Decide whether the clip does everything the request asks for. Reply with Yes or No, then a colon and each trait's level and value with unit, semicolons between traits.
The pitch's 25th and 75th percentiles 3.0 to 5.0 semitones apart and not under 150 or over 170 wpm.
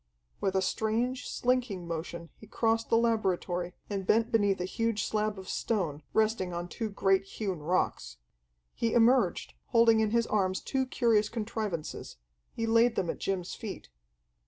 Yes: average, 3.5 semitones; average, 155 wpm